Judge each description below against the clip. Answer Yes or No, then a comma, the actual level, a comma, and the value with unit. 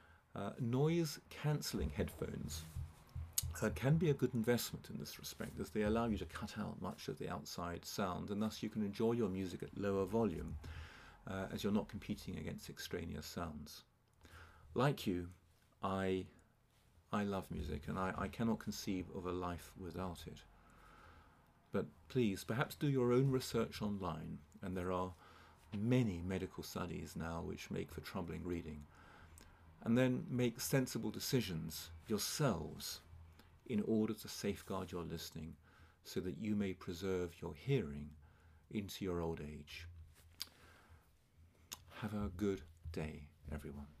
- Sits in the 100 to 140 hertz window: No, very low, 90 Hz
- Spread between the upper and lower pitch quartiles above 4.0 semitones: Yes, average, 4.5 semitones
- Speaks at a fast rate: No, average, 145 wpm